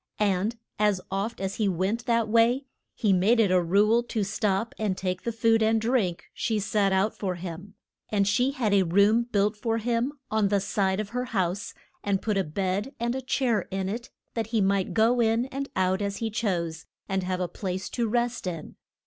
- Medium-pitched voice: No, high, 210 Hz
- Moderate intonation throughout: Yes, average, 3.3 semitones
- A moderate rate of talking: No, fast, 210 wpm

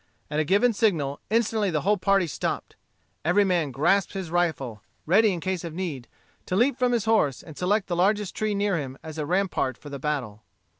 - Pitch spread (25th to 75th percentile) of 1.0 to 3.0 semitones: No, average, 5.3 semitones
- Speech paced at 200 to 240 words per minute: Yes, fast, 205 wpm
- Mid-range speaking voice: Yes, medium, 180 Hz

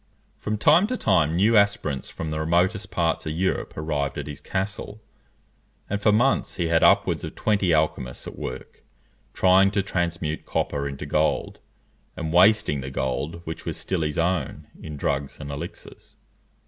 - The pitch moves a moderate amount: Yes, average, 4.6 semitones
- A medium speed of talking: Yes, average, 165 wpm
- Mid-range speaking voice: No, very low, 85 Hz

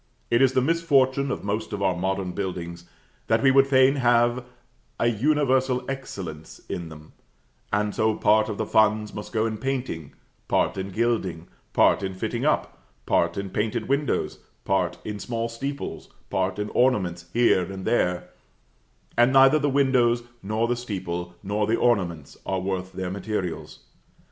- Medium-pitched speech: No, low, 110 Hz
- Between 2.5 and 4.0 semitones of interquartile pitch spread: No, average, 5.1 semitones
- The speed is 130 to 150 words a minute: No, average, 160 wpm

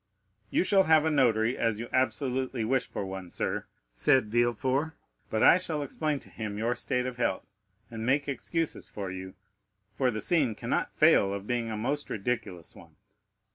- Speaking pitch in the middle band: No, low, 120 Hz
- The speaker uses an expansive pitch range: No, average, 4.5 semitones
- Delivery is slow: No, average, 175 wpm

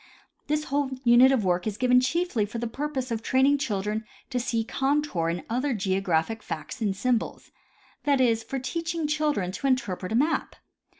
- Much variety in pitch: No, average, 4.9 semitones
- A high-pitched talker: Yes, very high, 250 Hz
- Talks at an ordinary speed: Yes, average, 180 wpm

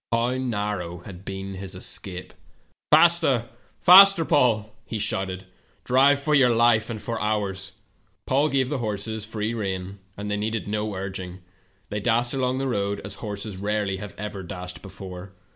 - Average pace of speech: Yes, average, 155 wpm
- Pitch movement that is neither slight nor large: Yes, average, 3.8 semitones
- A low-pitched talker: Yes, low, 105 Hz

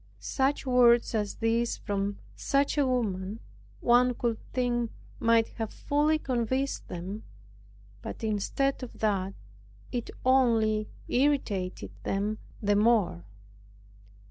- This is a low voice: No, high, 230 Hz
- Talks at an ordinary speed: No, slow, 110 wpm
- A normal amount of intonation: Yes, average, 3.5 semitones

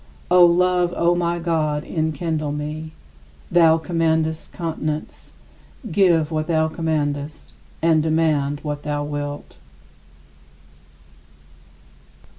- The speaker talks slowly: Yes, slow, 90 wpm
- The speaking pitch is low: No, medium, 160 Hz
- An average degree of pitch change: No, narrow, 2.1 semitones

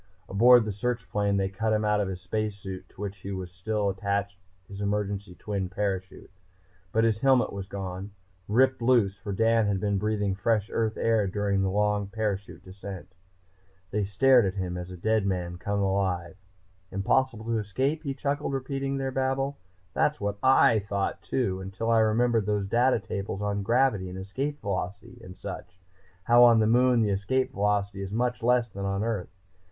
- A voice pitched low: Yes, low, 105 Hz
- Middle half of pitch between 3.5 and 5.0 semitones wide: No, average, 3.1 semitones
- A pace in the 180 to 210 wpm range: Yes, average, 185 wpm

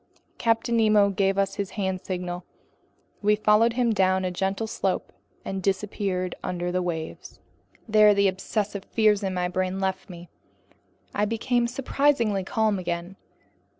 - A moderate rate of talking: Yes, average, 145 wpm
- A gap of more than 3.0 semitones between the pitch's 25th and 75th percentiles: No, narrow, 2.5 semitones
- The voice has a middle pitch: No, high, 195 Hz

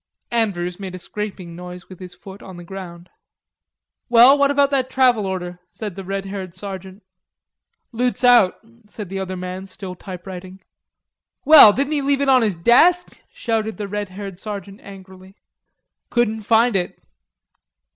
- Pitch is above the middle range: Yes, high, 195 Hz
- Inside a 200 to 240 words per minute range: No, average, 155 wpm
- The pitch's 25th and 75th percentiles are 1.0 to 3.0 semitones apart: No, average, 4.1 semitones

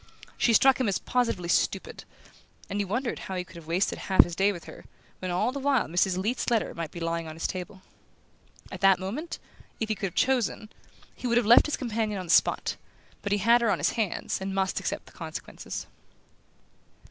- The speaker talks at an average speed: No, fast, 215 wpm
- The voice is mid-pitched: No, high, 200 Hz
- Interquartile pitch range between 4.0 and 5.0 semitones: Yes, average, 4.5 semitones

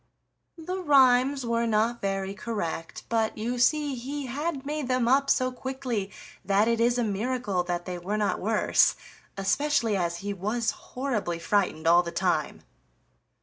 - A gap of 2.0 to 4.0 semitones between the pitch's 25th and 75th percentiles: No, average, 4.9 semitones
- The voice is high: Yes, high, 230 Hz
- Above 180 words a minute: No, average, 155 wpm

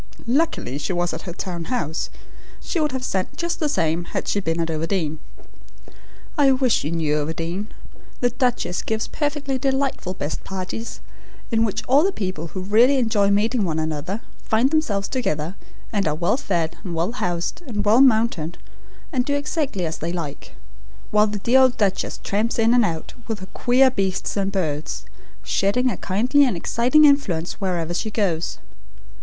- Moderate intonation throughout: No, wide, 6.7 semitones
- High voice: Yes, high, 205 Hz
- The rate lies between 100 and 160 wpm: No, average, 175 wpm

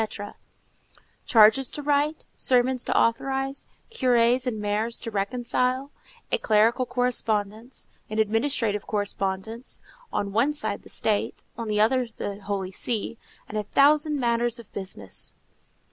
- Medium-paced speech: No, slow, 130 wpm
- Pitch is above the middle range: Yes, high, 230 Hz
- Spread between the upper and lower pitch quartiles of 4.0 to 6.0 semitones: No, average, 3.6 semitones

